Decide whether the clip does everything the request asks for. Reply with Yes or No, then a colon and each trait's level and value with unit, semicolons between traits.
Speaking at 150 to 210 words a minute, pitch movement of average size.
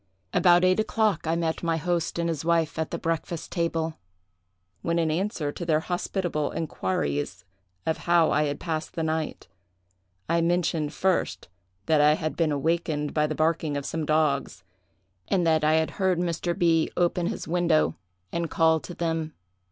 No: average, 170 wpm; narrow, 1.7 semitones